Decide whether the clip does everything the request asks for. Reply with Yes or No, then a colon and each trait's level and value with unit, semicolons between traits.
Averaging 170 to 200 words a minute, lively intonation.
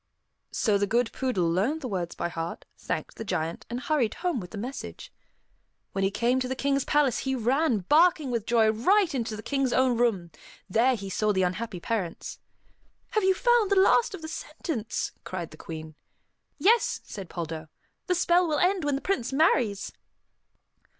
Yes: average, 185 wpm; wide, 7.6 semitones